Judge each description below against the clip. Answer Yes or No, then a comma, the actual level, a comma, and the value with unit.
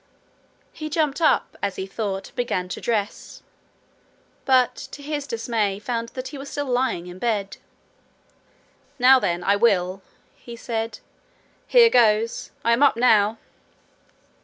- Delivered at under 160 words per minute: Yes, average, 140 wpm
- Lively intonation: No, average, 4.5 semitones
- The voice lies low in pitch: No, high, 230 Hz